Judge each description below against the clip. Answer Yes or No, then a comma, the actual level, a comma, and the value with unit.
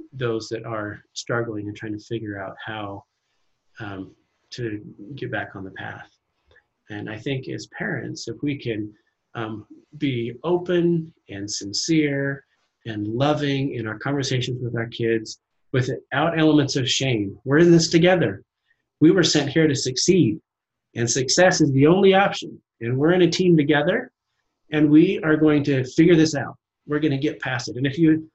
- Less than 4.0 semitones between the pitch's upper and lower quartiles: No, wide, 5.5 semitones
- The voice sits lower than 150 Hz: Yes, medium, 140 Hz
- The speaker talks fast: No, average, 170 wpm